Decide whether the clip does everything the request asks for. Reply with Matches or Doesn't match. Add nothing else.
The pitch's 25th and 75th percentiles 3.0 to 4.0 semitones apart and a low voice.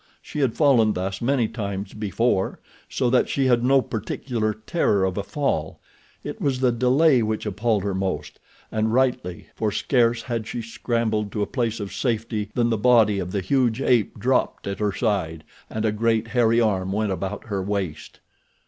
Matches